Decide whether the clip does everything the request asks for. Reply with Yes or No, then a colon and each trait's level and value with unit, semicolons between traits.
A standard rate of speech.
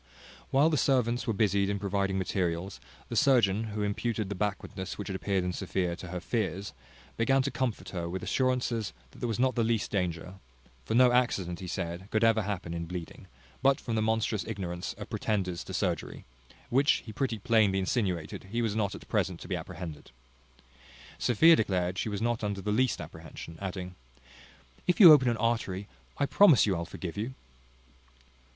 Yes: average, 185 wpm